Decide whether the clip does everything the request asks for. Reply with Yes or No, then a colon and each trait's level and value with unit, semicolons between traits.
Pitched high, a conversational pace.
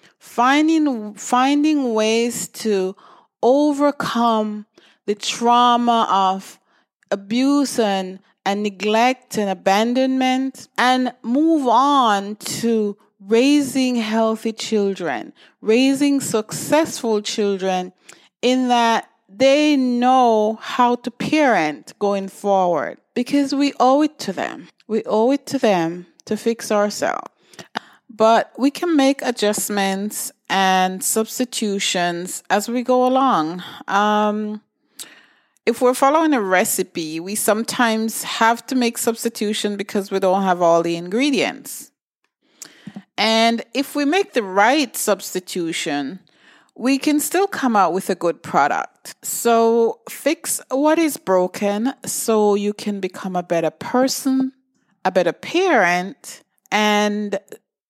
No: high, 225 Hz; slow, 115 wpm